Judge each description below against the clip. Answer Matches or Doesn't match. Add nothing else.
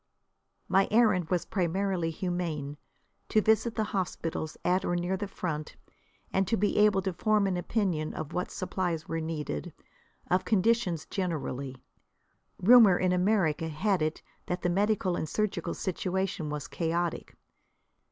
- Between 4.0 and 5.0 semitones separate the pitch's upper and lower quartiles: Doesn't match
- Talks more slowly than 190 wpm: Matches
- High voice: Doesn't match